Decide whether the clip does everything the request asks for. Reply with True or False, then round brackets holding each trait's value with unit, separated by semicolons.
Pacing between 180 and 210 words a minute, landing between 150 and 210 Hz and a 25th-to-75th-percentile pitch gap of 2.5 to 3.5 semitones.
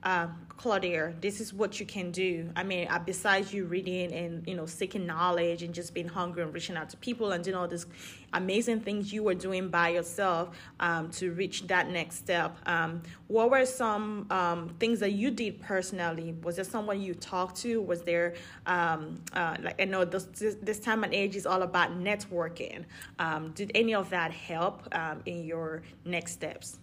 True (195 wpm; 185 Hz; 2.9 semitones)